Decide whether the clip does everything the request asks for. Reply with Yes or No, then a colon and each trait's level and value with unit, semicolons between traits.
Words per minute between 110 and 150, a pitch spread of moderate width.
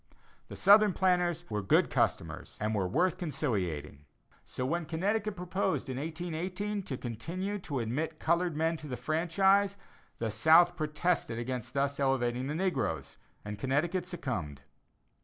No: average, 140 wpm; wide, 6.4 semitones